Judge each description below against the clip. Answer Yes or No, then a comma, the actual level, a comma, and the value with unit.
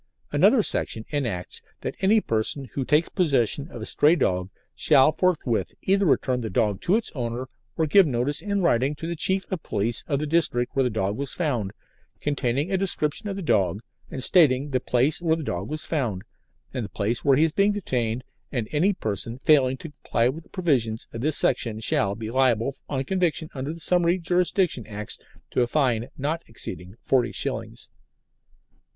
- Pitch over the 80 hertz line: Yes, low, 135 Hz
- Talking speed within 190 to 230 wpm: Yes, average, 195 wpm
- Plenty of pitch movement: Yes, wide, 5.9 semitones